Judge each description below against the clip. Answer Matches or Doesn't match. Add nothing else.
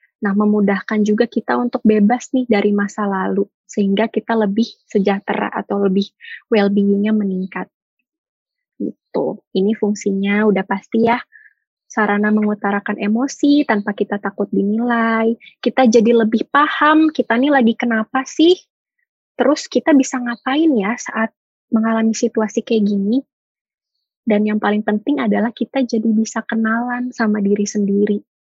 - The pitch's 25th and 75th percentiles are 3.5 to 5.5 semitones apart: Doesn't match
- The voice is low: Doesn't match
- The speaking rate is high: Doesn't match